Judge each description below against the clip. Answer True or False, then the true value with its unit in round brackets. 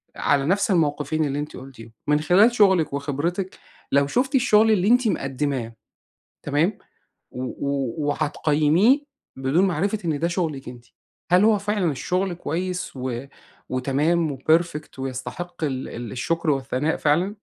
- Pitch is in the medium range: True (155 Hz)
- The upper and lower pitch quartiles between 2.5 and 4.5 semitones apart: False (5.0 semitones)